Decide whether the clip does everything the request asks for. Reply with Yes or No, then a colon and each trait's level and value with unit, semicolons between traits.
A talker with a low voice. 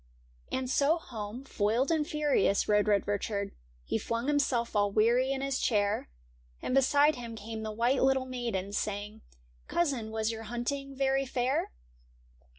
No: high, 240 Hz